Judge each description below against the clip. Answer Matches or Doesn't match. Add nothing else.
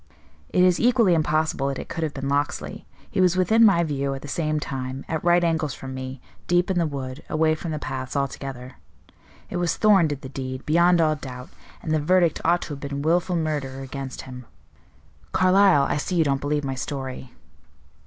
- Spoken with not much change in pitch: Doesn't match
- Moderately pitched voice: Matches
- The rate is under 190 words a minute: Doesn't match